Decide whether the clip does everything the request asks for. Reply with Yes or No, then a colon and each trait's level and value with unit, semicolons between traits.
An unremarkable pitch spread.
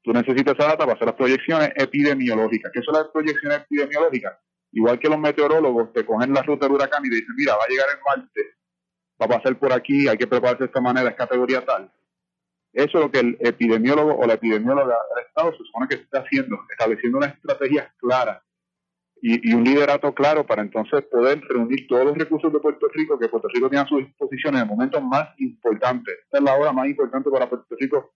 Yes: average, 3.8 semitones